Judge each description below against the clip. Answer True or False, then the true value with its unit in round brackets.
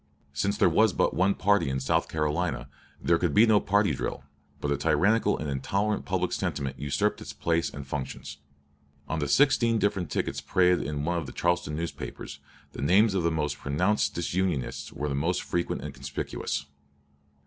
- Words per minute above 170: True (180 wpm)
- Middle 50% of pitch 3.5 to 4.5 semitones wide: False (5.3 semitones)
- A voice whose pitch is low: True (85 Hz)